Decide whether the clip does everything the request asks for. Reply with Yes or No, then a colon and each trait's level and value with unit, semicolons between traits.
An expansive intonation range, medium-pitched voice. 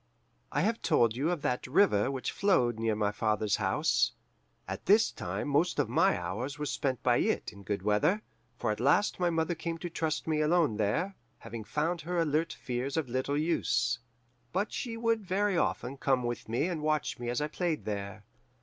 Yes: wide, 6.7 semitones; medium, 145 Hz